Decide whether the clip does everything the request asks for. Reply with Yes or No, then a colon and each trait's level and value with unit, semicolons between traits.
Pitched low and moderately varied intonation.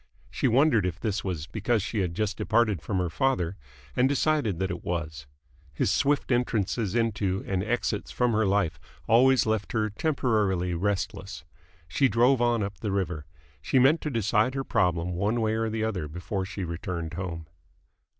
Yes: low, 105 Hz; average, 4.7 semitones